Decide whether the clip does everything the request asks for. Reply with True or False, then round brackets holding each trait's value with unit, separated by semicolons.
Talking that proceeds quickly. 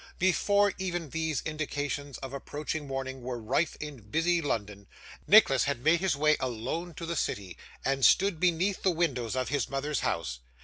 False (170 wpm)